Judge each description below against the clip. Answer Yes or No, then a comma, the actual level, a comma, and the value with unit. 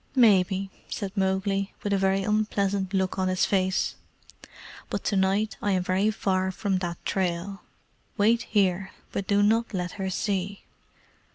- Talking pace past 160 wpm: No, average, 155 wpm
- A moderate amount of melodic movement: No, narrow, 1.4 semitones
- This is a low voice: No, high, 195 Hz